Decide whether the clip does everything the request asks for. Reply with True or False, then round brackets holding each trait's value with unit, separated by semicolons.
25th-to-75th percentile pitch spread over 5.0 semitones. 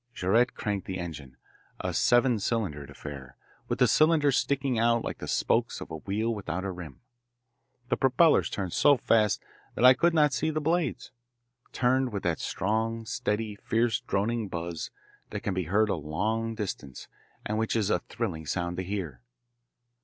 True (5.4 semitones)